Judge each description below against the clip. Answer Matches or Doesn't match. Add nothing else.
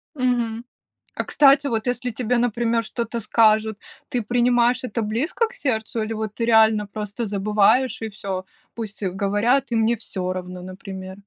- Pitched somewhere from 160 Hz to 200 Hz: Doesn't match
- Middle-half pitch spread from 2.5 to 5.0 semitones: Matches